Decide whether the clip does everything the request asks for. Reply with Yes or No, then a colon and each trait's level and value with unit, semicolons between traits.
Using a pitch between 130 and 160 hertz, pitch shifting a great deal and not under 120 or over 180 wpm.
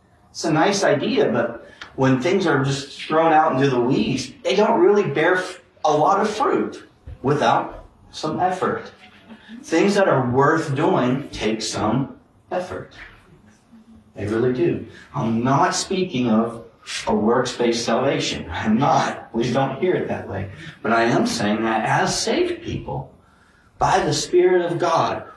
Yes: low, 135 Hz; wide, 7.4 semitones; average, 150 wpm